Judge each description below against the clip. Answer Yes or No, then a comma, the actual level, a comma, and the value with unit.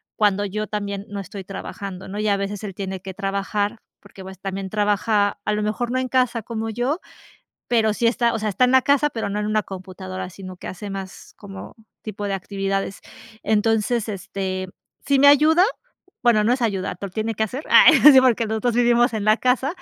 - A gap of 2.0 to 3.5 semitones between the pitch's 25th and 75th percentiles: Yes, average, 3.2 semitones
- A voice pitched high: Yes, high, 210 Hz